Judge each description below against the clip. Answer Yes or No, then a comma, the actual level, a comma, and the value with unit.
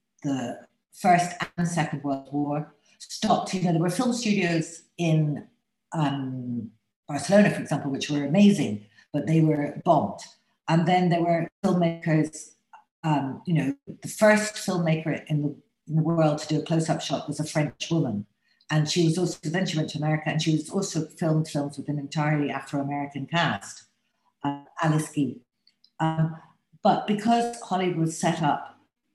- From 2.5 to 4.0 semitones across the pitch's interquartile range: Yes, average, 3.4 semitones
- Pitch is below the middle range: No, medium, 160 Hz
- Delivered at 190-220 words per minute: No, average, 165 wpm